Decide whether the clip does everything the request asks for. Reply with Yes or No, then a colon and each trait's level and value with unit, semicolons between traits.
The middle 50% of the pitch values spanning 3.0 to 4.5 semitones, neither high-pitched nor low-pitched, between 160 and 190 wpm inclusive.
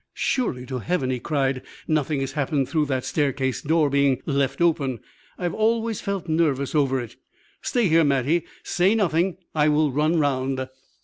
Yes: average, 3.9 semitones; medium, 150 Hz; average, 165 wpm